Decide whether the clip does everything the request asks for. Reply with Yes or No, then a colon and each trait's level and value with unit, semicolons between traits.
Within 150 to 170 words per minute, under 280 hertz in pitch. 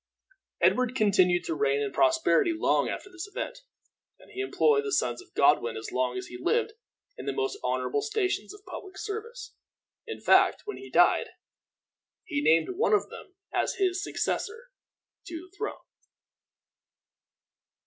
No: average, 155 wpm; very high, 370 Hz